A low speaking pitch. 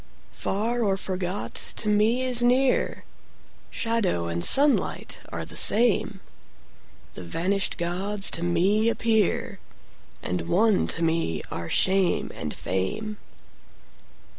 No: high, 195 Hz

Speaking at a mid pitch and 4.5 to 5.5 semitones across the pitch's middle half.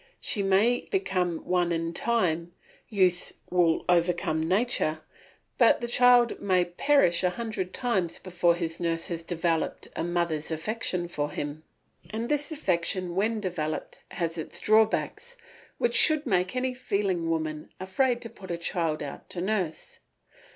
Yes: medium, 180 Hz; average, 4.8 semitones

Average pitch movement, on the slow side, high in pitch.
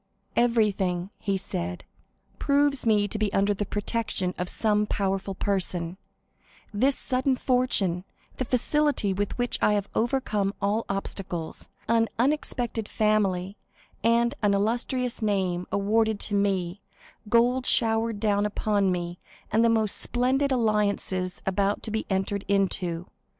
Yes: average, 3.1 semitones; slow, 130 wpm; high, 210 Hz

